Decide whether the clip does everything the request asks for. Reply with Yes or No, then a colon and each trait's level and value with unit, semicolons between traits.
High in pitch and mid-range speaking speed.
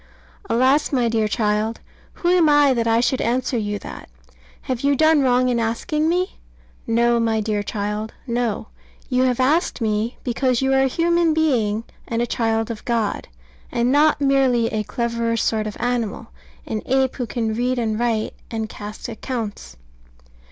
Yes: high, 235 Hz; average, 170 wpm